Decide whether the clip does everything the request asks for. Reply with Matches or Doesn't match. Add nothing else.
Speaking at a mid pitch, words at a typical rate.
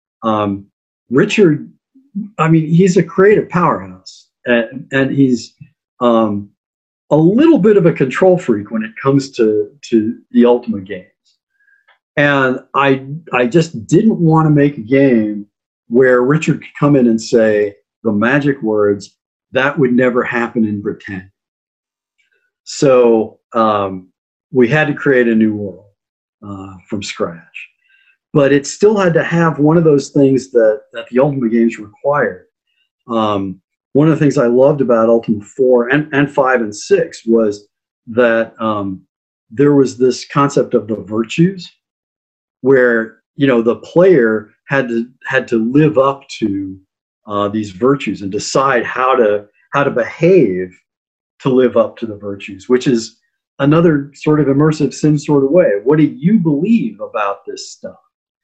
Doesn't match